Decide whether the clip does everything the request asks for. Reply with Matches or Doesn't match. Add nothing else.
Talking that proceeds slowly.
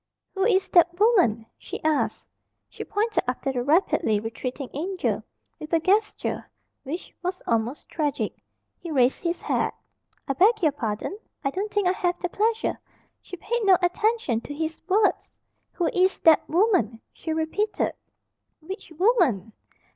Doesn't match